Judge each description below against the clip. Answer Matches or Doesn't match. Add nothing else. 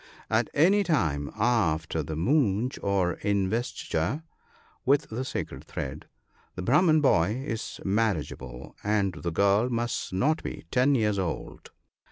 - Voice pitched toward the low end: Matches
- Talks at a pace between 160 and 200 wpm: Doesn't match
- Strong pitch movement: Matches